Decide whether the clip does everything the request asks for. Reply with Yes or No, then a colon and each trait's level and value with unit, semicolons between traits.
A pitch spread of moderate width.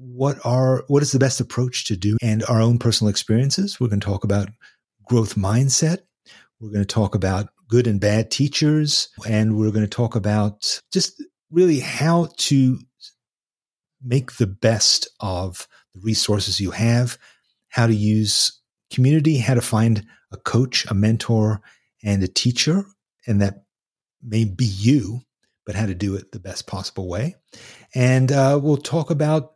Yes: average, 4.3 semitones